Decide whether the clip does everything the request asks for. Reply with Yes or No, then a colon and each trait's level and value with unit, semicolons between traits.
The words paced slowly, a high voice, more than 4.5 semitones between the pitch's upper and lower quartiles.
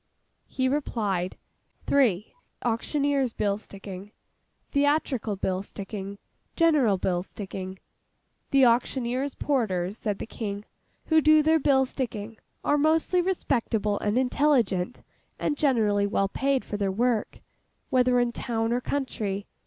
Yes: slow, 120 wpm; high, 235 Hz; wide, 5.5 semitones